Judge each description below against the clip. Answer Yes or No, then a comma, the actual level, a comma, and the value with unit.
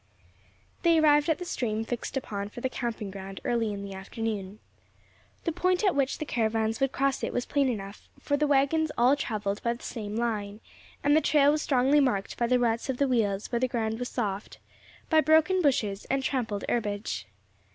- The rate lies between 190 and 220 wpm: Yes, average, 195 wpm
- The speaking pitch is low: No, high, 240 Hz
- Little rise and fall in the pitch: No, average, 5.0 semitones